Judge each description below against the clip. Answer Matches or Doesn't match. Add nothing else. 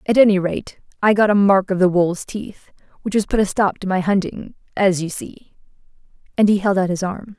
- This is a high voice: Matches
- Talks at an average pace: Doesn't match